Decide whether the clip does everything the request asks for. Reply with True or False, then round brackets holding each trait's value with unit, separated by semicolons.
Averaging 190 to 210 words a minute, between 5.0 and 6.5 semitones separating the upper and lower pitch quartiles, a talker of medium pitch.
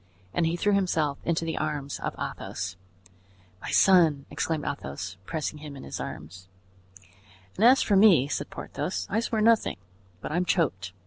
False (165 wpm; 5.3 semitones; 160 Hz)